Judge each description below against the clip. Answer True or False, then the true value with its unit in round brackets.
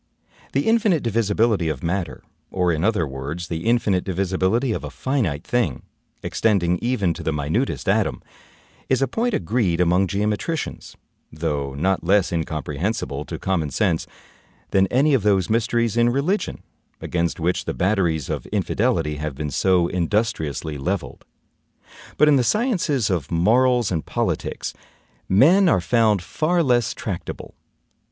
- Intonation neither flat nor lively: False (6.2 semitones)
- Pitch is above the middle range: False (95 Hz)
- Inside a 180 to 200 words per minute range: False (145 wpm)